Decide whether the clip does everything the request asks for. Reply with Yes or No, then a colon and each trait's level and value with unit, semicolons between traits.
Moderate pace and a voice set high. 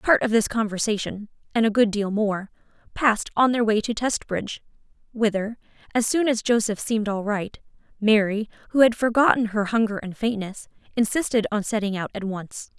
Yes: average, 175 wpm; high, 215 Hz